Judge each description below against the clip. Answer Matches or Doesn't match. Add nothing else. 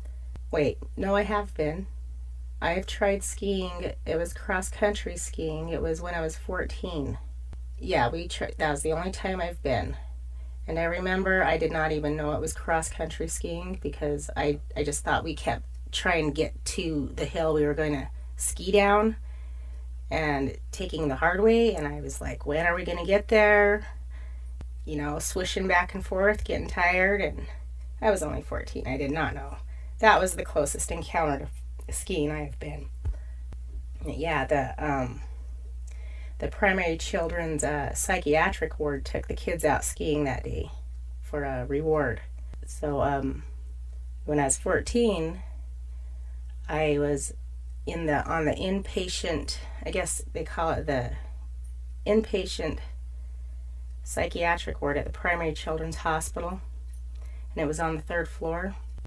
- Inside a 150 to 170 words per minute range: Matches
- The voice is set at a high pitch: Doesn't match